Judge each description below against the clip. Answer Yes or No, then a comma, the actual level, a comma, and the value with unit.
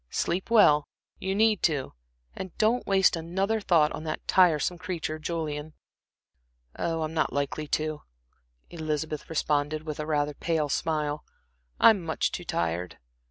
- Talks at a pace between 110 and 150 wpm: Yes, average, 140 wpm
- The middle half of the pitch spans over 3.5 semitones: No, average, 3.0 semitones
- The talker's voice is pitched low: No, medium, 155 Hz